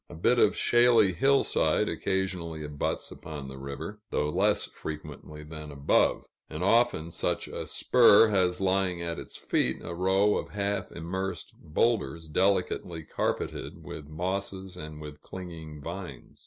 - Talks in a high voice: No, very low, 90 Hz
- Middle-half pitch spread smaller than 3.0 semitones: No, average, 4.0 semitones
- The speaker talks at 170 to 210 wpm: No, average, 140 wpm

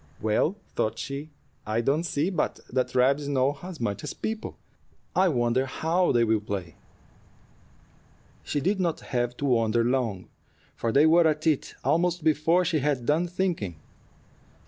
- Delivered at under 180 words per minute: Yes, average, 155 wpm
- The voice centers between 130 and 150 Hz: Yes, medium, 140 Hz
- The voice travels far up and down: Yes, wide, 5.7 semitones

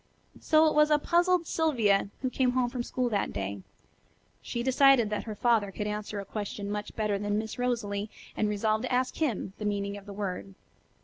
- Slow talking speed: No, average, 200 wpm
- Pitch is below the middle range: No, high, 215 Hz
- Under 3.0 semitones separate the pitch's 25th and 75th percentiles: No, average, 3.8 semitones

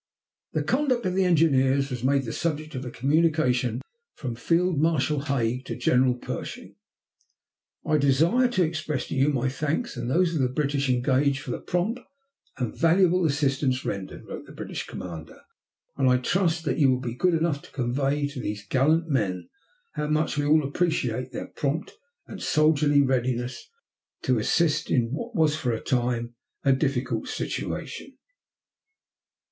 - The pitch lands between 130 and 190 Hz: Yes, medium, 140 Hz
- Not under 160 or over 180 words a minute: Yes, average, 165 wpm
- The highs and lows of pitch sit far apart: No, average, 4.0 semitones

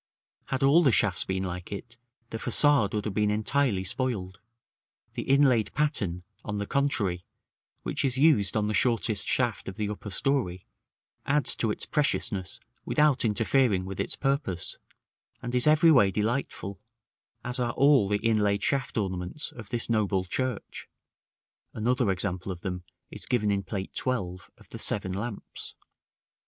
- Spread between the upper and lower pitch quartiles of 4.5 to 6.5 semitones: Yes, average, 5.0 semitones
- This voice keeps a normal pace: Yes, average, 155 wpm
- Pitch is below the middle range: Yes, low, 110 Hz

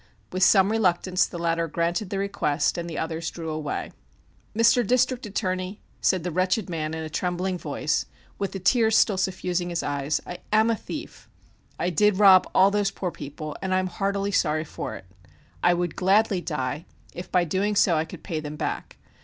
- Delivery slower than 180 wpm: No, average, 195 wpm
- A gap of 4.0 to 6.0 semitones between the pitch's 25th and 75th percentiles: No, average, 3.4 semitones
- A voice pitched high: No, medium, 180 Hz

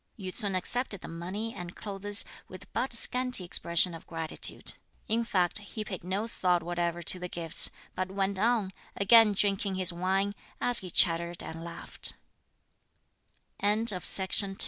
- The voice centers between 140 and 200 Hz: Yes, high, 190 Hz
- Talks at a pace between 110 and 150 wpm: Yes, average, 145 wpm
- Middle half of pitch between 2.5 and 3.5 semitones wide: Yes, average, 3.0 semitones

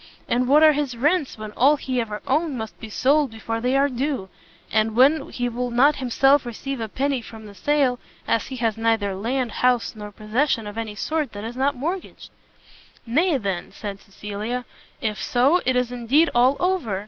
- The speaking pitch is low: No, high, 245 Hz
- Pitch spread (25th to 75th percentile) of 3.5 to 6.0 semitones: Yes, average, 4.0 semitones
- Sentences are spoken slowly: No, average, 195 wpm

